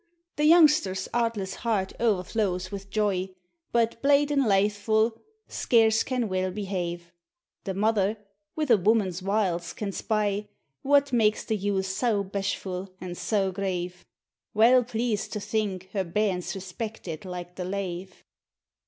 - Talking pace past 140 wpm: No, slow, 135 wpm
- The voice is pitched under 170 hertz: No, high, 200 Hz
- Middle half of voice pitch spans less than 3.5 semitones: Yes, average, 3.0 semitones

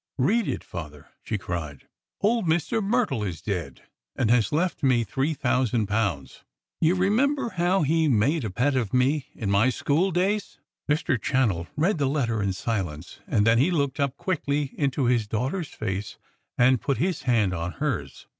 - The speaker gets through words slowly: No, average, 175 wpm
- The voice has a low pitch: Yes, low, 130 Hz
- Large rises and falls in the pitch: Yes, wide, 7.6 semitones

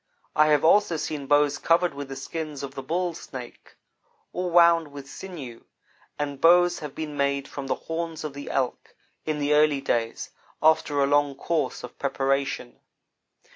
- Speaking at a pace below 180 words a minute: Yes, average, 170 wpm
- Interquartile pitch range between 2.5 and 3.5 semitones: Yes, average, 2.9 semitones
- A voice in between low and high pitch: Yes, medium, 145 Hz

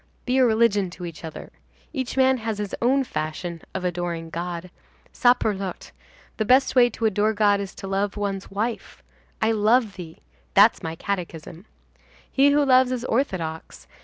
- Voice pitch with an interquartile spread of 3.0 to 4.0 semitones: No, wide, 5.4 semitones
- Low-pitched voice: No, high, 205 Hz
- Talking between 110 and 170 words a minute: Yes, average, 160 wpm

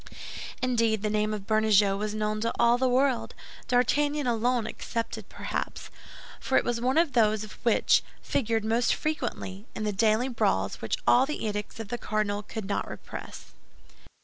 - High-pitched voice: Yes, high, 225 Hz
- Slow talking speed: No, average, 165 wpm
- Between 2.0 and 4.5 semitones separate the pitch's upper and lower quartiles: Yes, narrow, 2.6 semitones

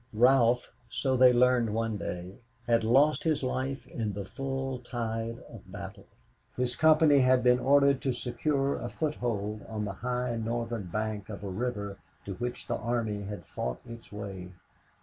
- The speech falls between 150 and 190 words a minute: Yes, average, 165 wpm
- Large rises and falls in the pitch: No, average, 3.5 semitones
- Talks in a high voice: No, low, 120 Hz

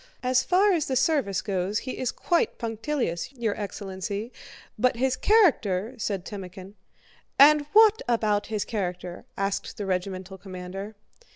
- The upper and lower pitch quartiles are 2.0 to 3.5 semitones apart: No, average, 5.3 semitones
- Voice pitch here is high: Yes, high, 210 Hz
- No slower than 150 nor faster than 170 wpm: No, slow, 135 wpm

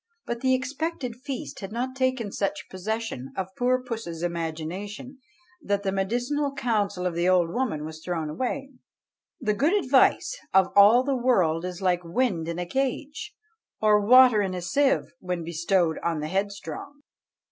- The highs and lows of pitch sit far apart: Yes, wide, 6.4 semitones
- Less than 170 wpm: Yes, average, 160 wpm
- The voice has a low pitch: No, high, 205 Hz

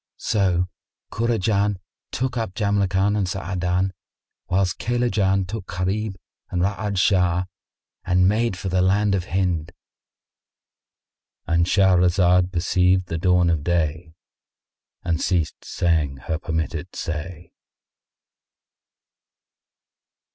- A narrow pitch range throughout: Yes, narrow, 2.2 semitones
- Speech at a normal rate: No, slow, 95 wpm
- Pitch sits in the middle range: No, very low, 90 Hz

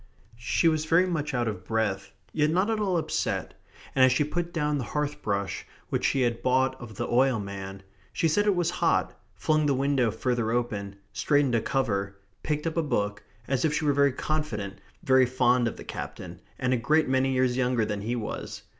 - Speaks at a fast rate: Yes, fast, 210 wpm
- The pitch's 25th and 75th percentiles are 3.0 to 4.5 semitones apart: No, average, 5.1 semitones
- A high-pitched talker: No, low, 130 Hz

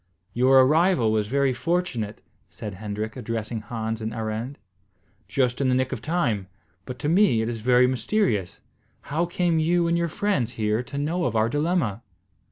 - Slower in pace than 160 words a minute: No, average, 175 wpm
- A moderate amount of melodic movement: No, wide, 6.2 semitones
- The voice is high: No, low, 125 Hz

